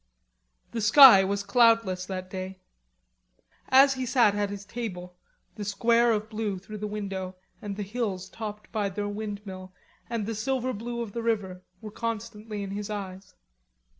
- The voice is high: Yes, high, 210 Hz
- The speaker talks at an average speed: Yes, average, 165 wpm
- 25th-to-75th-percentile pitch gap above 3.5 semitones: No, average, 2.8 semitones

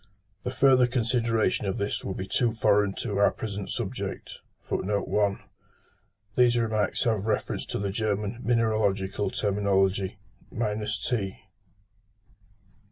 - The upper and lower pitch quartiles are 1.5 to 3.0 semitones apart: Yes, narrow, 2.6 semitones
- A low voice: Yes, low, 105 Hz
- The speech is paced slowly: Yes, slow, 105 wpm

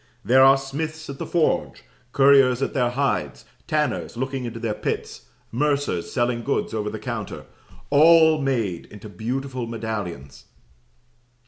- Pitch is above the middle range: No, low, 130 Hz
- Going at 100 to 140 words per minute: Yes, slow, 135 wpm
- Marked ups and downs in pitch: No, average, 3.9 semitones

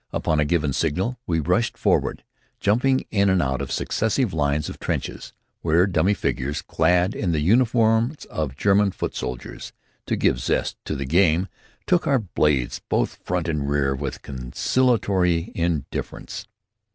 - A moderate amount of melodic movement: No, wide, 5.9 semitones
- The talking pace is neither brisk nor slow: Yes, average, 150 wpm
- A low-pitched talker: Yes, very low, 85 Hz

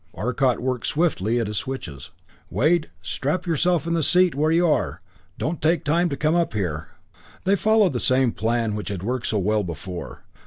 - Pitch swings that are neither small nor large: No, wide, 7.9 semitones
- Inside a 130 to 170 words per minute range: No, average, 190 wpm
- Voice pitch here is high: No, low, 130 Hz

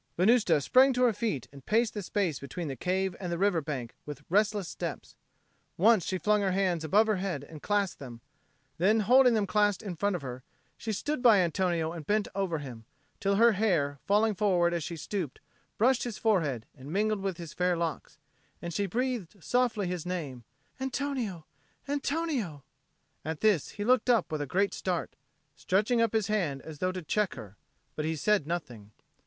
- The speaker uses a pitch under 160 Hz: No, high, 190 Hz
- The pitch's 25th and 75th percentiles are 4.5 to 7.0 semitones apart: Yes, average, 5.1 semitones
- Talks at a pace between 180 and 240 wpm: Yes, average, 190 wpm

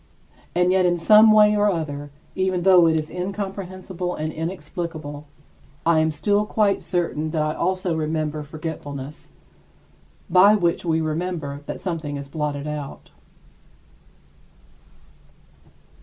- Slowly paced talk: Yes, slow, 125 wpm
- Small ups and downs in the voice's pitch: No, average, 3.5 semitones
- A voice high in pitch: No, medium, 170 Hz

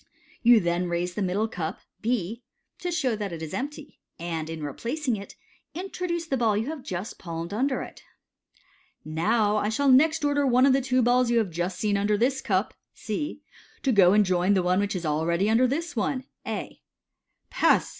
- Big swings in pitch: Yes, wide, 6.6 semitones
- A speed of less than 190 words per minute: No, average, 195 wpm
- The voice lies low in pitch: No, high, 220 Hz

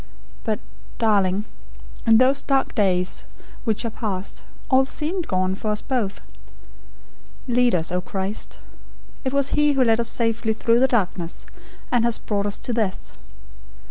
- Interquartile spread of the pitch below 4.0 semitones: No, average, 4.3 semitones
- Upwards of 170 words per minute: No, average, 150 wpm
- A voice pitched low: No, high, 225 Hz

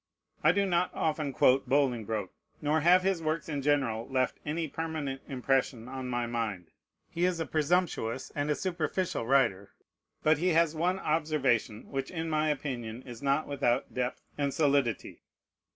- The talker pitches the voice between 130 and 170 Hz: Yes, medium, 140 Hz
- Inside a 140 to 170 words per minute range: Yes, average, 160 wpm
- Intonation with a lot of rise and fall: No, average, 4.3 semitones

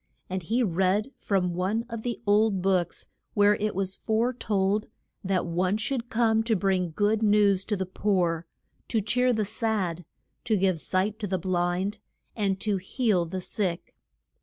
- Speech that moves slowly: No, average, 165 wpm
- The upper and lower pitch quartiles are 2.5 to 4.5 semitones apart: Yes, average, 2.9 semitones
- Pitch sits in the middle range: No, high, 200 Hz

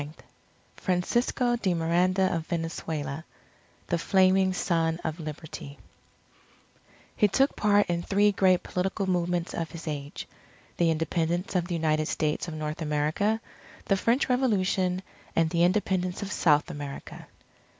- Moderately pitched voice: Yes, medium, 175 Hz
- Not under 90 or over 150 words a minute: Yes, average, 140 wpm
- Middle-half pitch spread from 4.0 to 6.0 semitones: No, average, 3.1 semitones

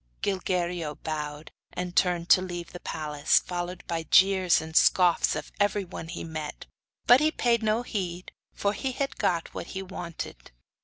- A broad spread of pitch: No, average, 3.0 semitones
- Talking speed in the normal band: Yes, average, 165 wpm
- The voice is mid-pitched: Yes, medium, 180 Hz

